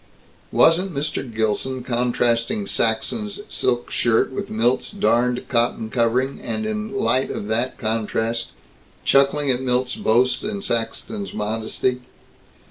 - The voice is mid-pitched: No, low, 125 Hz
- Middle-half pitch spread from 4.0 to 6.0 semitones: No, average, 3.4 semitones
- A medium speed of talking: No, slow, 120 wpm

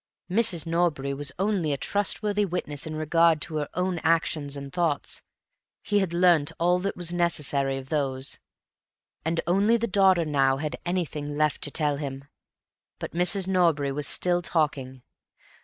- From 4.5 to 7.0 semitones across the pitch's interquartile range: No, average, 3.8 semitones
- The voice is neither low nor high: Yes, medium, 165 Hz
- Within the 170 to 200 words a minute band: No, average, 155 wpm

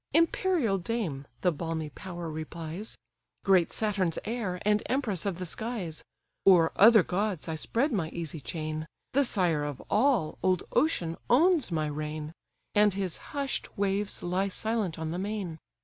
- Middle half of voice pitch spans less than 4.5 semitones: No, average, 5.1 semitones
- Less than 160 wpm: Yes, average, 150 wpm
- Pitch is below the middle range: No, medium, 185 Hz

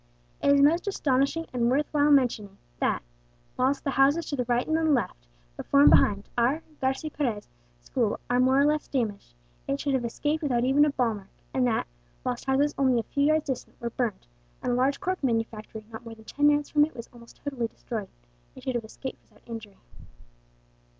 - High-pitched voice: Yes, very high, 260 Hz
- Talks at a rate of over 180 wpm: Yes, fast, 205 wpm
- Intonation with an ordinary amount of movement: Yes, average, 3.9 semitones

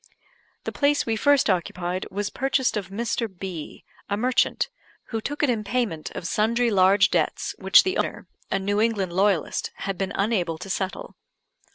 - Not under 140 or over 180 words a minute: Yes, average, 170 wpm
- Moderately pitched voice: No, high, 205 Hz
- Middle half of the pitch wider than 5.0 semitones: No, average, 3.7 semitones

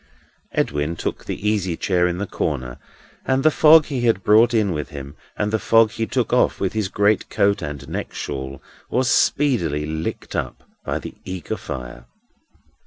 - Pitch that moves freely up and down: Yes, wide, 7.2 semitones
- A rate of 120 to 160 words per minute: No, average, 175 wpm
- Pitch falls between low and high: No, very low, 95 Hz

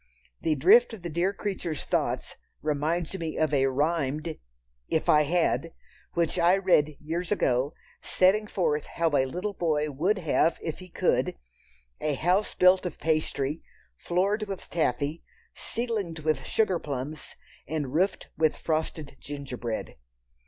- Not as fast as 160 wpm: Yes, average, 140 wpm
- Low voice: No, medium, 160 Hz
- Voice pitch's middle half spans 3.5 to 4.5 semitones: Yes, average, 3.8 semitones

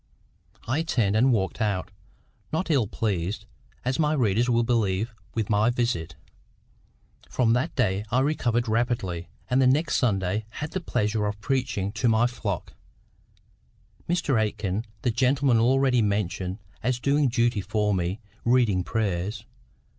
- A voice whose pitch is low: Yes, low, 115 Hz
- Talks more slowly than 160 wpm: Yes, average, 140 wpm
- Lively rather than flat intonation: No, average, 3.9 semitones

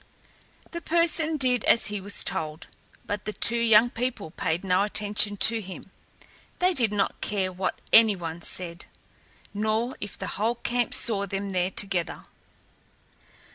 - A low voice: No, high, 210 Hz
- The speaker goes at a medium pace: Yes, average, 150 wpm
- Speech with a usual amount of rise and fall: Yes, average, 3.9 semitones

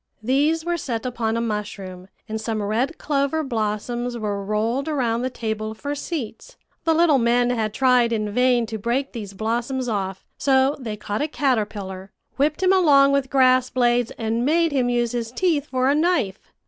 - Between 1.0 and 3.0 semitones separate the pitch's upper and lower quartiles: No, average, 4.1 semitones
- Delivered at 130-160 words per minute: No, average, 180 wpm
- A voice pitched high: Yes, high, 245 Hz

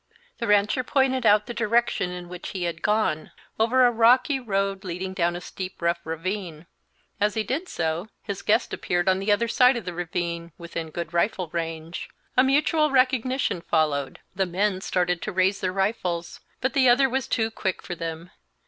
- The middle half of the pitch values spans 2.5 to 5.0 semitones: No, wide, 5.4 semitones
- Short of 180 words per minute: No, average, 185 wpm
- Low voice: No, high, 195 Hz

